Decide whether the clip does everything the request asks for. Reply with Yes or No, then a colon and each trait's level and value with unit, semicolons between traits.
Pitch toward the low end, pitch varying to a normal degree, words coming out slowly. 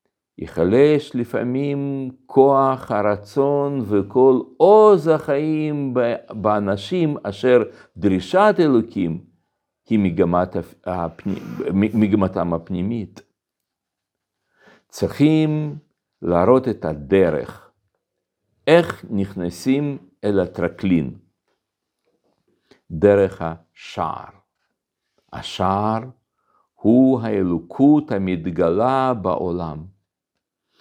No: low, 105 Hz; wide, 6.4 semitones; slow, 55 wpm